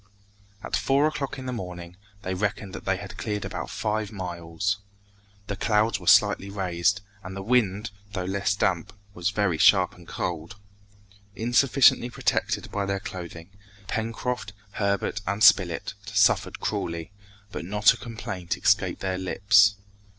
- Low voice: Yes, low, 100 Hz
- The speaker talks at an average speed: Yes, average, 145 wpm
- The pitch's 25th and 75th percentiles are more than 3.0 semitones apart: No, narrow, 2.5 semitones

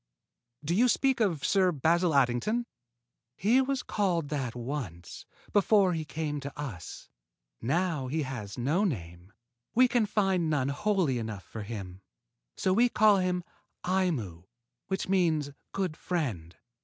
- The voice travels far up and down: Yes, wide, 7.5 semitones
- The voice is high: No, medium, 160 Hz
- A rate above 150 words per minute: No, average, 145 wpm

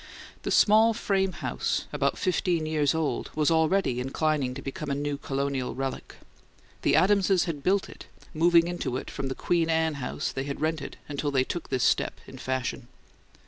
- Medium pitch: Yes, medium, 155 Hz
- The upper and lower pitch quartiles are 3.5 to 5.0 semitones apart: Yes, average, 4.2 semitones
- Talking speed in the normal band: Yes, average, 180 wpm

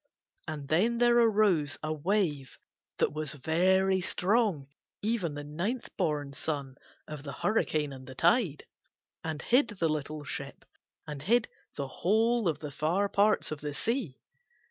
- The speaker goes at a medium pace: Yes, average, 150 wpm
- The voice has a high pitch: No, medium, 160 Hz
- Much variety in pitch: Yes, wide, 6.1 semitones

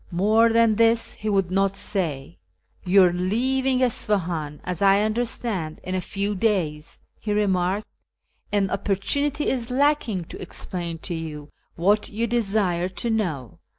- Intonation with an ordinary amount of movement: Yes, average, 4.3 semitones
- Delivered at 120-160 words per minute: Yes, average, 150 wpm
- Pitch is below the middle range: No, high, 200 Hz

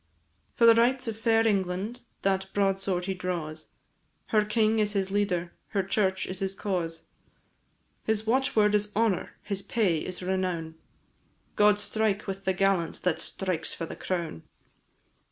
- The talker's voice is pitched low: No, high, 195 Hz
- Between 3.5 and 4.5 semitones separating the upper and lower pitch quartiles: No, average, 2.7 semitones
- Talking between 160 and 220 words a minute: No, average, 150 wpm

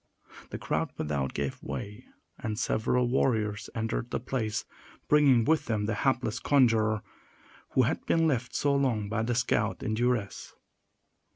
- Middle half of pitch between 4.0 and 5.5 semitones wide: No, average, 3.0 semitones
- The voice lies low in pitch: Yes, low, 115 Hz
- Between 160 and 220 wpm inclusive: No, average, 150 wpm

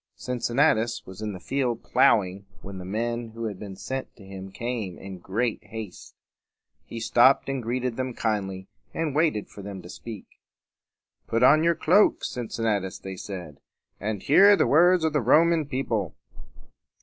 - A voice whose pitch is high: No, low, 115 Hz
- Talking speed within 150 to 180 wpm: Yes, average, 160 wpm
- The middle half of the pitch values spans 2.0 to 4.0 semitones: No, average, 5.1 semitones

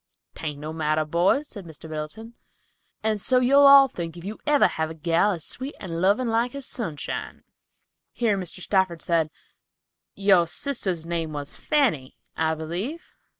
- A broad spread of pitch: Yes, wide, 6.6 semitones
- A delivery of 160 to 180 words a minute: Yes, average, 165 wpm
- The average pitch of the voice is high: No, medium, 180 Hz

